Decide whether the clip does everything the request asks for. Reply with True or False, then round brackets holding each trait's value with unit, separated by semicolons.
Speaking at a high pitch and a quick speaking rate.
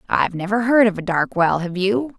True (195 Hz; 245 wpm)